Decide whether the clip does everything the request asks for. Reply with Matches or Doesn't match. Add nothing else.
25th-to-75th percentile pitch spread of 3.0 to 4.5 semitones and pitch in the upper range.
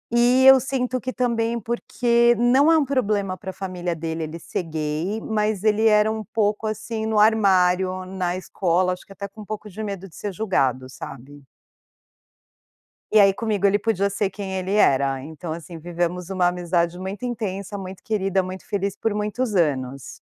Matches